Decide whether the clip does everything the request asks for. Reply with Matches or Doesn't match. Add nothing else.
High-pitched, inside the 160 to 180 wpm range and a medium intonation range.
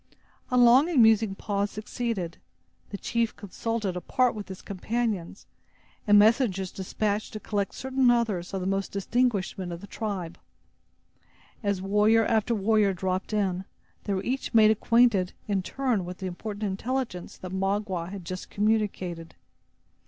Doesn't match